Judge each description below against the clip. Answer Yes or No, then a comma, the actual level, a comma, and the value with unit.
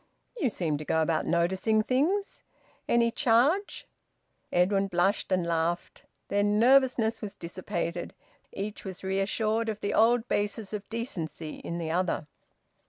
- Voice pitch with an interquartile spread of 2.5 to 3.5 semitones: No, average, 4.8 semitones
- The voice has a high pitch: Yes, high, 205 Hz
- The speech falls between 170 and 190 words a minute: No, slow, 135 wpm